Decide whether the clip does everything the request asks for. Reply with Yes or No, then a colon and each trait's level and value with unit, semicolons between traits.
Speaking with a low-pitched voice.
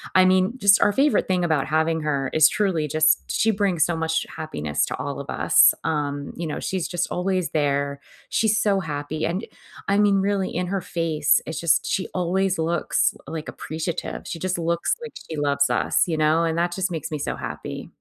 No: medium, 165 Hz